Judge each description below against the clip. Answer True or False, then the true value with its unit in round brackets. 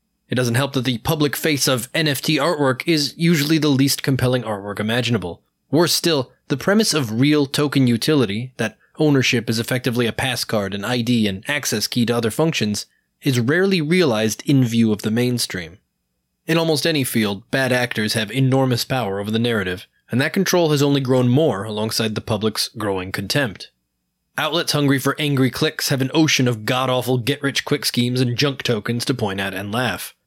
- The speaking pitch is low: True (130 Hz)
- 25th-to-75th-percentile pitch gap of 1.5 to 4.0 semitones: False (4.4 semitones)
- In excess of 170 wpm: True (180 wpm)